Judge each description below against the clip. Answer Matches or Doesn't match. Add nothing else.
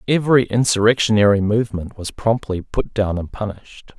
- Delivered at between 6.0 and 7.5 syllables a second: Doesn't match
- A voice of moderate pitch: Doesn't match